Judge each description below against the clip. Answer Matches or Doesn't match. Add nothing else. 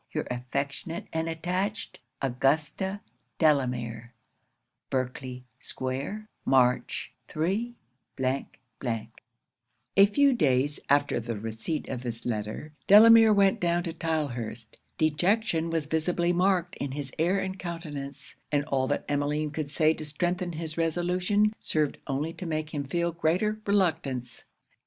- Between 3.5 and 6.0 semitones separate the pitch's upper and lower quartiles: Matches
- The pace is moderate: Doesn't match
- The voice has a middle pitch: Matches